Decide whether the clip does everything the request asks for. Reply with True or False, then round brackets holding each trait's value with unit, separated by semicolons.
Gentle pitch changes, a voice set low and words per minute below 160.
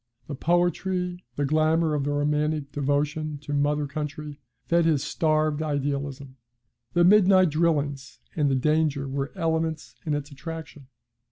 False (2.1 semitones; 150 Hz; 140 wpm)